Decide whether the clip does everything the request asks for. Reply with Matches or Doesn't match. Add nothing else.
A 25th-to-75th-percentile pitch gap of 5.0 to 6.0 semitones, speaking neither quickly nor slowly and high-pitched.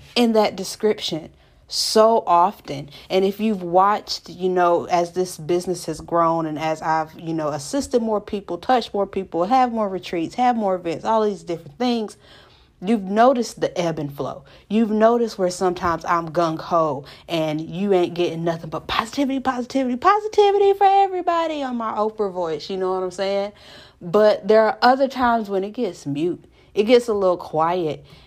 Matches